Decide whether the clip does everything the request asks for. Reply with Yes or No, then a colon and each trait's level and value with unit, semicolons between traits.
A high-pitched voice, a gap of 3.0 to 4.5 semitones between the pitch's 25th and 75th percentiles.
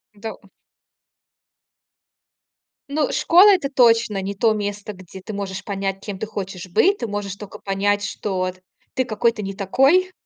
Yes: high, 205 Hz; average, 3.3 semitones